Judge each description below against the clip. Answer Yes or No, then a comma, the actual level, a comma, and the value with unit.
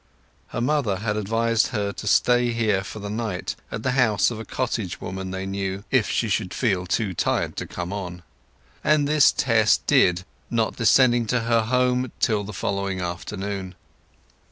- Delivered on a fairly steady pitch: No, average, 3.6 semitones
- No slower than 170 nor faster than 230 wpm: Yes, average, 175 wpm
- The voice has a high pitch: No, low, 105 Hz